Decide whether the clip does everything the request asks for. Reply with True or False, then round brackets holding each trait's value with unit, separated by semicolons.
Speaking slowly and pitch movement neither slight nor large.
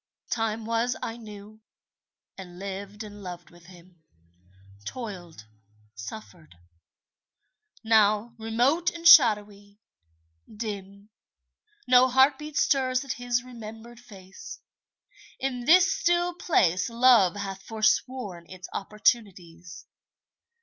True (95 wpm; 4.3 semitones)